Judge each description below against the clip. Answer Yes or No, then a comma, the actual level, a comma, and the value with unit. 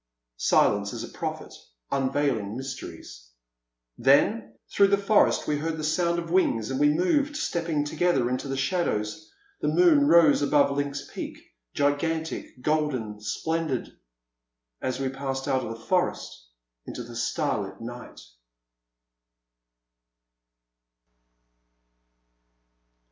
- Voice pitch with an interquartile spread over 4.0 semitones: Yes, average, 4.6 semitones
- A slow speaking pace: Yes, slow, 120 wpm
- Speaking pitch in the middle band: Yes, medium, 145 Hz